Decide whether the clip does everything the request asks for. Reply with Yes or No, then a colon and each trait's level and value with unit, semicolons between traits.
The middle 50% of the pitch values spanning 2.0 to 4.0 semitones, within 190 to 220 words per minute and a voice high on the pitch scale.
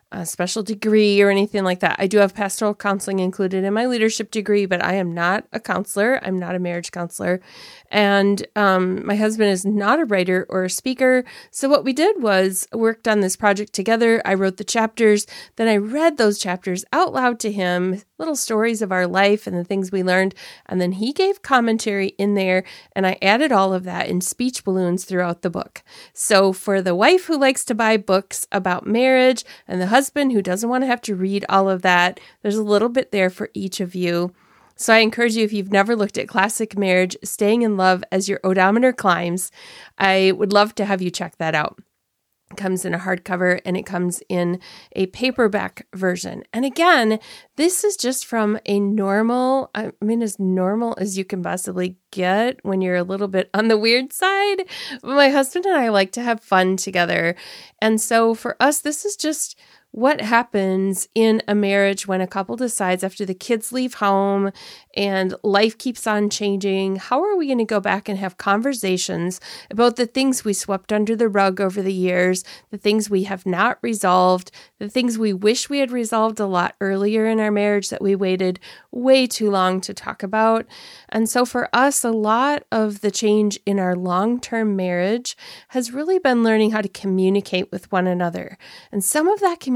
Yes: average, 3.6 semitones; fast, 205 wpm; high, 205 Hz